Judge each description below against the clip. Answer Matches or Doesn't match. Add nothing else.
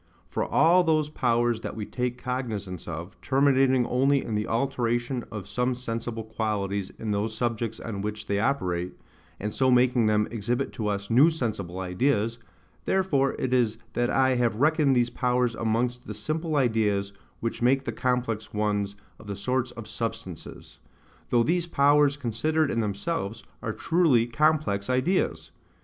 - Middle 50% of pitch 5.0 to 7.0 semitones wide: Doesn't match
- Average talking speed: Matches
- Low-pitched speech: Matches